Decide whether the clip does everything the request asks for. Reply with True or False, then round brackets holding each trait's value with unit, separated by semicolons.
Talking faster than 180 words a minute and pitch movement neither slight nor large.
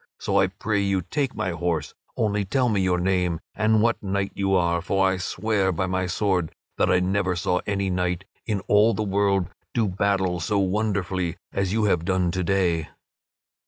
False (190 wpm; 2.0 semitones)